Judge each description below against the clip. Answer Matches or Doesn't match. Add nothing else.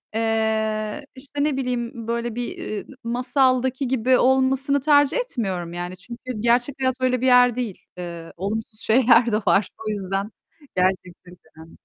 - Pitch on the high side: Matches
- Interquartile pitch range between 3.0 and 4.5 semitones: Matches